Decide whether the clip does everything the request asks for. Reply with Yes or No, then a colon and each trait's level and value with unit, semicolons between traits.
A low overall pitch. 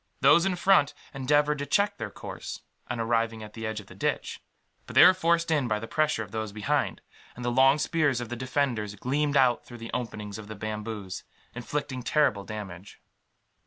Yes: low, 120 Hz